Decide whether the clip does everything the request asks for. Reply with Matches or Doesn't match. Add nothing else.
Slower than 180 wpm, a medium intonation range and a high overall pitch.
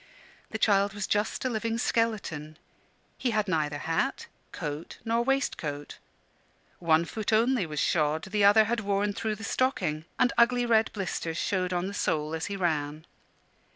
Doesn't match